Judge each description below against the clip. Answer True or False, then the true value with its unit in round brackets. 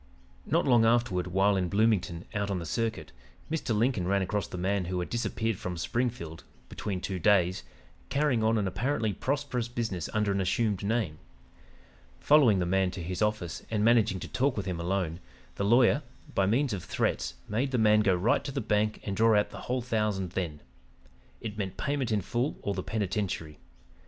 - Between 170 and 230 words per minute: True (190 wpm)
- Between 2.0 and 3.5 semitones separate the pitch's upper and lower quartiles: False (4.0 semitones)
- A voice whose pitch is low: True (105 Hz)